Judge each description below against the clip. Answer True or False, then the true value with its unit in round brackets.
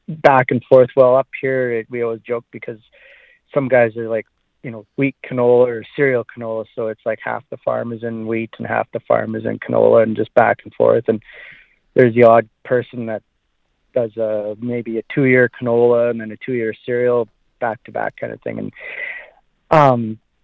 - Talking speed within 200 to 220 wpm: True (205 wpm)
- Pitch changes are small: True (2.2 semitones)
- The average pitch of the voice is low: True (120 Hz)